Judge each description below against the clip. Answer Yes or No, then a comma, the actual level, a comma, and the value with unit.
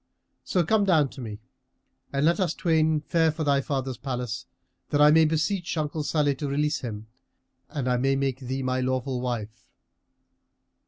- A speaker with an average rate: Yes, average, 170 wpm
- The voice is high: No, medium, 140 Hz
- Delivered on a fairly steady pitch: No, average, 3.6 semitones